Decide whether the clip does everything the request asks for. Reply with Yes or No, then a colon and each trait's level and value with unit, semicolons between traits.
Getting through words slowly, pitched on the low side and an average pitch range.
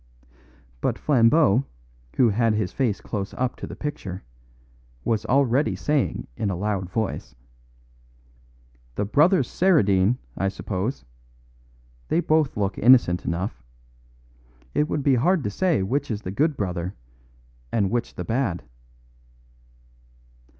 No: slow, 125 wpm; low, 115 Hz; wide, 6.2 semitones